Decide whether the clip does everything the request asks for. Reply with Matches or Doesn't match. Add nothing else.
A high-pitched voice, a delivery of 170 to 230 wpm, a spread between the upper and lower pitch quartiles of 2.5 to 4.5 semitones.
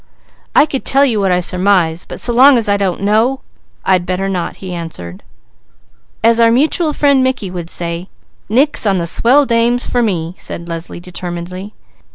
Doesn't match